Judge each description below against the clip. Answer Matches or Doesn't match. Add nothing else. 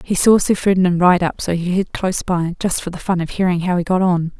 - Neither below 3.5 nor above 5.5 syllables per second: Doesn't match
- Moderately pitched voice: Matches